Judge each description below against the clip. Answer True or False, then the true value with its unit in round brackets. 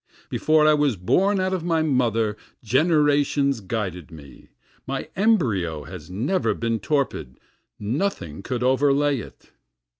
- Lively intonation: True (7.7 semitones)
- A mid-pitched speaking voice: False (130 Hz)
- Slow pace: True (125 wpm)